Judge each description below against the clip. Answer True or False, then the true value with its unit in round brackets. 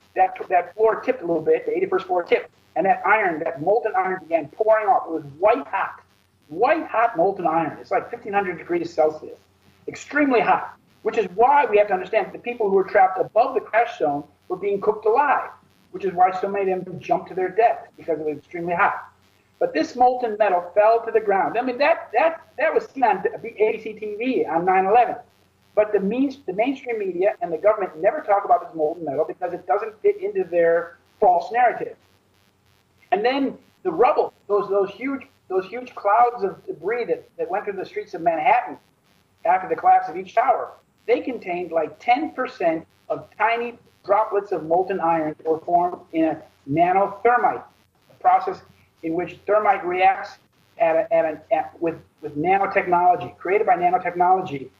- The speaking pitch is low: False (225 Hz)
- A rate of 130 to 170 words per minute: False (190 wpm)